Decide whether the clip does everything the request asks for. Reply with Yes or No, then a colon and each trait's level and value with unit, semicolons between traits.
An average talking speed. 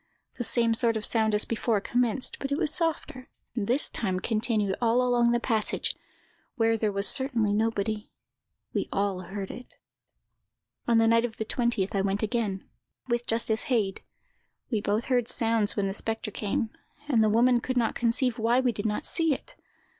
Yes: average, 185 wpm